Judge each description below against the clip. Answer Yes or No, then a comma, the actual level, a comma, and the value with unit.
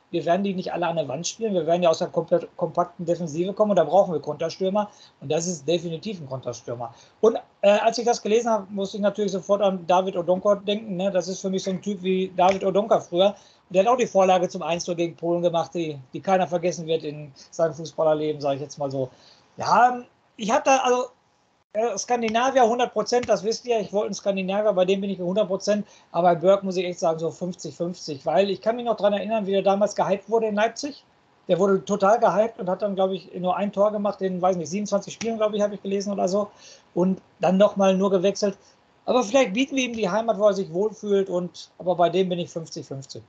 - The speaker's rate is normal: No, fast, 240 wpm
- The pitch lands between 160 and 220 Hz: Yes, high, 190 Hz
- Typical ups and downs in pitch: Yes, average, 3.2 semitones